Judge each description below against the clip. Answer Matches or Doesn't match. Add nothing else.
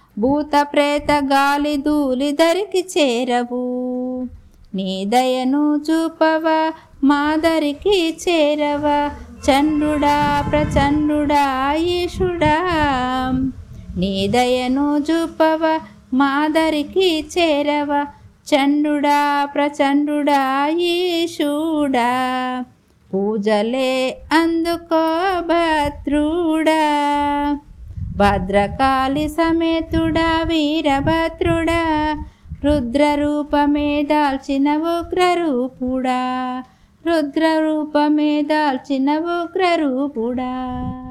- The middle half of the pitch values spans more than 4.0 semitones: Doesn't match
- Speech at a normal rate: Doesn't match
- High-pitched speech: Matches